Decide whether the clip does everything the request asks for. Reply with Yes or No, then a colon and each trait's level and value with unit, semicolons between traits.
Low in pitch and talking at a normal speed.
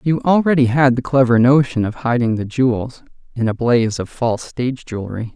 Yes: low, 125 Hz; average, 190 wpm